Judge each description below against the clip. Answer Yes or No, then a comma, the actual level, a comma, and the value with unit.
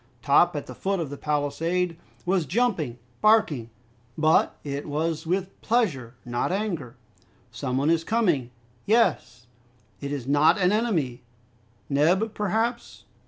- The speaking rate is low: Yes, slow, 130 wpm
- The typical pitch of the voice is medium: Yes, medium, 165 Hz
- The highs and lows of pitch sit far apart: Yes, wide, 5.8 semitones